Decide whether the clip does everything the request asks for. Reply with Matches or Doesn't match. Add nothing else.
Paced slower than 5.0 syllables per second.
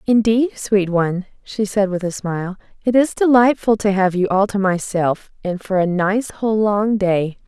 Matches